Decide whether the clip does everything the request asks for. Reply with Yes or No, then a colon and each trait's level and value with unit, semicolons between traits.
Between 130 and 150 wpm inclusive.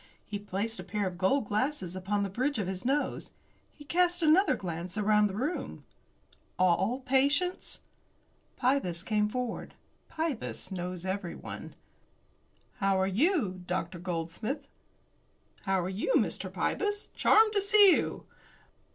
Yes: slow, 135 wpm